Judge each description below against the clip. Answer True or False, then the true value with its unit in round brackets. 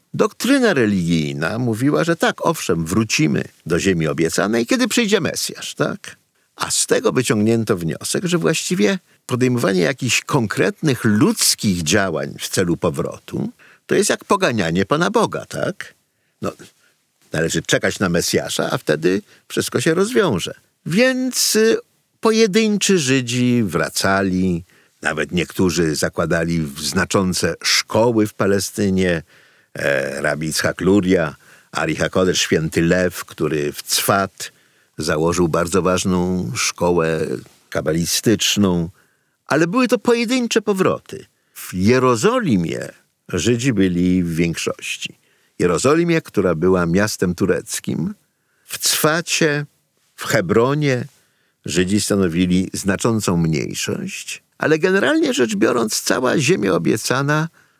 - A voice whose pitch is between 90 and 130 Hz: True (115 Hz)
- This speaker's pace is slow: True (105 wpm)